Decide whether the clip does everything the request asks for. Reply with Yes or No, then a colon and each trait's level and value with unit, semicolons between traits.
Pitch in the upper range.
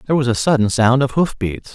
No: low, 125 Hz